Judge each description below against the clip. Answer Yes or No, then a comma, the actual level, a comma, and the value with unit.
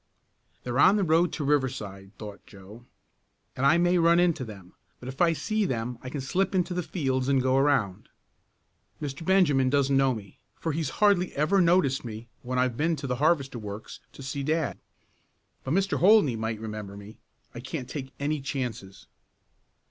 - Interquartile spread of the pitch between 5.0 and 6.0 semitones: Yes, wide, 5.5 semitones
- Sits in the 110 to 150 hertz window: Yes, low, 135 Hz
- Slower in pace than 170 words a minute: No, average, 180 wpm